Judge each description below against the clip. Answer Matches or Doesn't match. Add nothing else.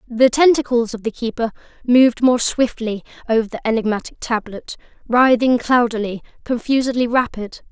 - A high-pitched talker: Matches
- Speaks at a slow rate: Matches